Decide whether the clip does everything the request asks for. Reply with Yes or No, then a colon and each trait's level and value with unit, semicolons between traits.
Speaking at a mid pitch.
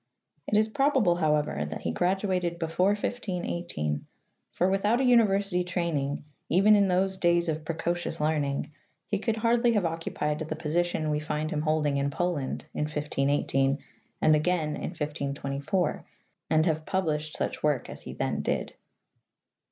Yes: medium, 165 Hz